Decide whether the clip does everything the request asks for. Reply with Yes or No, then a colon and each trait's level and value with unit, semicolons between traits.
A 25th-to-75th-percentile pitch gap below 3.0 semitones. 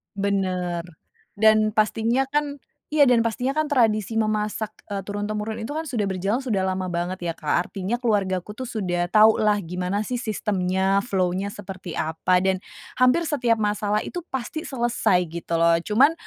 No: average, 3.8 semitones